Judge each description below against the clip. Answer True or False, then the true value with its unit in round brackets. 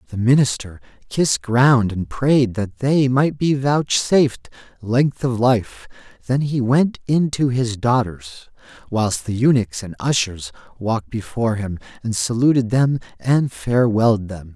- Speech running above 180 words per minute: False (145 wpm)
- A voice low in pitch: True (120 Hz)